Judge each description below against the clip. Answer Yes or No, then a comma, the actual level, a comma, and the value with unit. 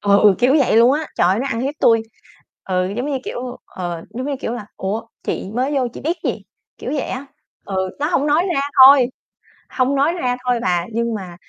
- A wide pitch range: Yes, wide, 5.7 semitones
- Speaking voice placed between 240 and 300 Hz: Yes, high, 245 Hz